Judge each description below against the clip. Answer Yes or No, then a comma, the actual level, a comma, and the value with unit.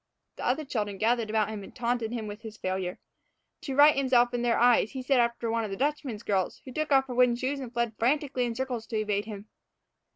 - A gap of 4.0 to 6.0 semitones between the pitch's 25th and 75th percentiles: No, average, 3.2 semitones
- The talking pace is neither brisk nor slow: No, fast, 235 wpm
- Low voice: No, high, 235 Hz